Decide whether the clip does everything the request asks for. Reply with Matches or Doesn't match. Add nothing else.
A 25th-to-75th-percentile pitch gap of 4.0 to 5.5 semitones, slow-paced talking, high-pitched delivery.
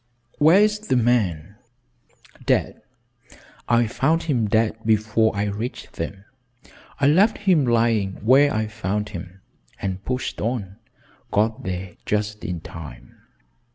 Doesn't match